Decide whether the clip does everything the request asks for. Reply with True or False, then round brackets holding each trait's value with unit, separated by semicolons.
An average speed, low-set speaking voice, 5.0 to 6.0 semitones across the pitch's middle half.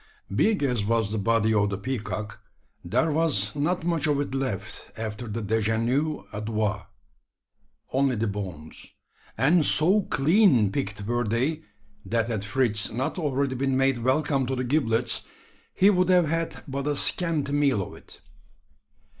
True (155 wpm; 125 Hz; 5.3 semitones)